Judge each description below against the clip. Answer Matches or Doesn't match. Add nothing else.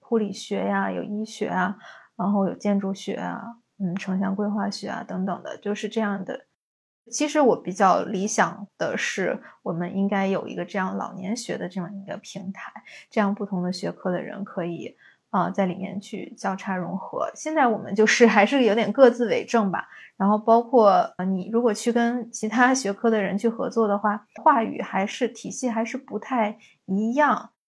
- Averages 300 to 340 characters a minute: Doesn't match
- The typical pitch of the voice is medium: Doesn't match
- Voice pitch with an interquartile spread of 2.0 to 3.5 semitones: Matches